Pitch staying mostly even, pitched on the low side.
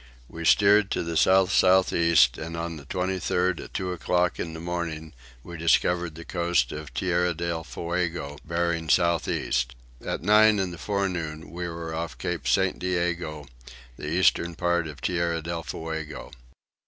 Yes: narrow, 1.7 semitones; very low, 85 Hz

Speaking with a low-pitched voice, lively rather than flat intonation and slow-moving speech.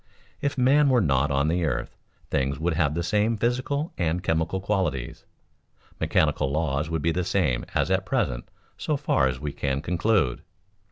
No: very low, 85 Hz; wide, 6.9 semitones; average, 170 wpm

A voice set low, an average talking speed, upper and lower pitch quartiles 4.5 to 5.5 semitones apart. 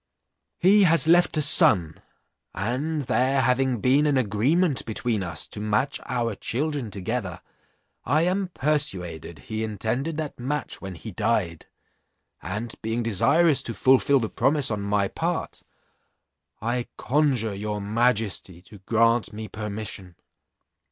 No: low, 115 Hz; slow, 130 wpm; average, 5.2 semitones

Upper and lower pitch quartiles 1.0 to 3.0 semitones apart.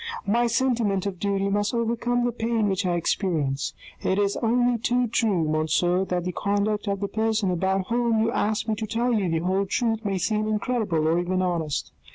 No: average, 3.7 semitones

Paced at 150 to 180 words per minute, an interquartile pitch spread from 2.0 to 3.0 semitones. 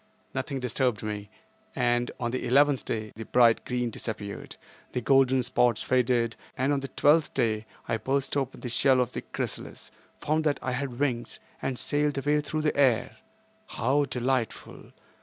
Yes: average, 165 wpm; average, 2.7 semitones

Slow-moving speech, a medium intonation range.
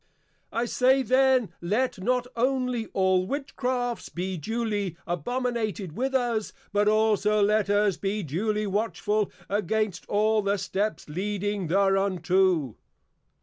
Yes: slow, 115 wpm; average, 3.7 semitones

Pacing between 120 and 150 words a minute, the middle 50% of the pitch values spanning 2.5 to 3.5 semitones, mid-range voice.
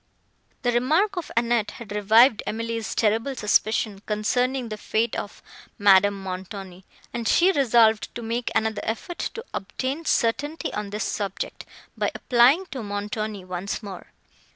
No: average, 140 wpm; average, 3.2 semitones; high, 220 Hz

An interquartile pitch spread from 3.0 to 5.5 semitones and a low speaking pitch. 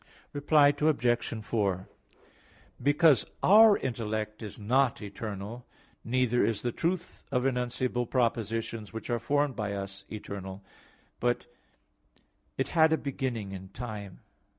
Yes: average, 4.3 semitones; low, 120 Hz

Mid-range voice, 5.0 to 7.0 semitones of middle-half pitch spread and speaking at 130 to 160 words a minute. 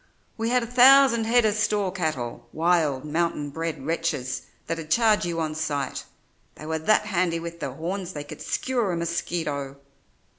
No: medium, 170 Hz; wide, 5.5 semitones; average, 170 wpm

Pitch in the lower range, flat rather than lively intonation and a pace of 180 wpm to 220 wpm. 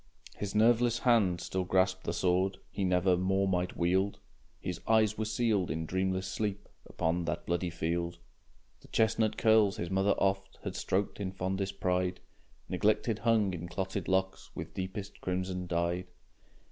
No: very low, 95 Hz; narrow, 2.1 semitones; average, 155 wpm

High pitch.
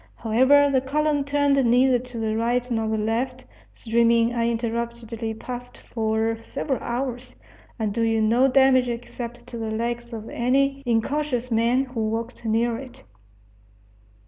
Yes: high, 235 Hz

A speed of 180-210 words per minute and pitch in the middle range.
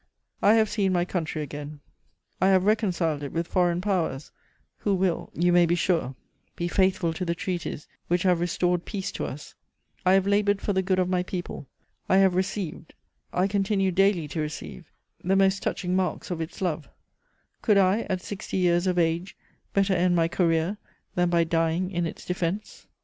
Yes: average, 185 wpm; medium, 180 Hz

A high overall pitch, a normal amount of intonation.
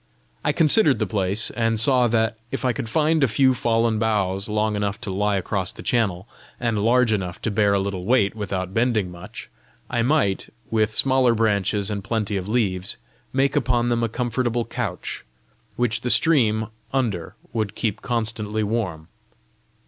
No: low, 110 Hz; average, 3.1 semitones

